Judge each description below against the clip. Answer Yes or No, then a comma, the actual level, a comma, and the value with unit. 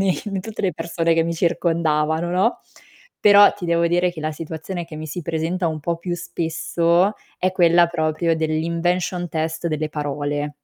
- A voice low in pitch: No, medium, 170 Hz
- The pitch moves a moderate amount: No, narrow, 1.9 semitones